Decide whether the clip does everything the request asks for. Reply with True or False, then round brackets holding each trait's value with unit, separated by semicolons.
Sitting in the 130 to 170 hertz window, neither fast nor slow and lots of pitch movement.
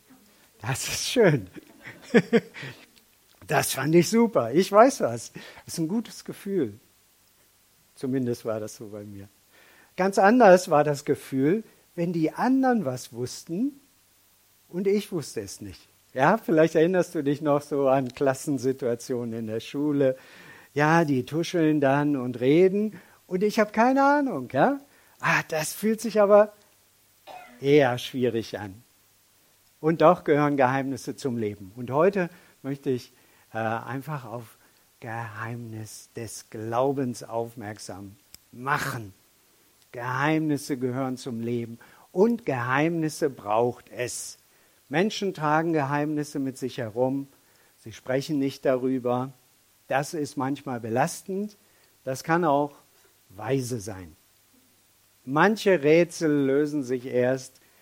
False (135 Hz; 120 wpm; 5.9 semitones)